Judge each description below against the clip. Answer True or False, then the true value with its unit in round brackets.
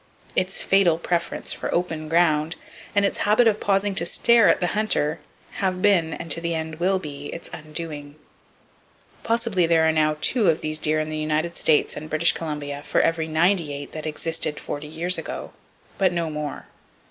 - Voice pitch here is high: False (165 Hz)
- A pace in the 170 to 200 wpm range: True (180 wpm)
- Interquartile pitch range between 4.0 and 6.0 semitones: False (3.0 semitones)